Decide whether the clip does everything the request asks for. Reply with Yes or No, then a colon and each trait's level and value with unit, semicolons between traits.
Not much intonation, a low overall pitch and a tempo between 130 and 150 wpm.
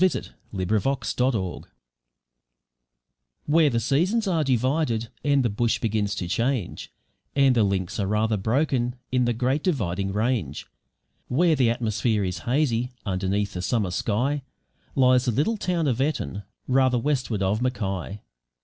No: average, 4.9 semitones; low, 120 Hz; average, 140 wpm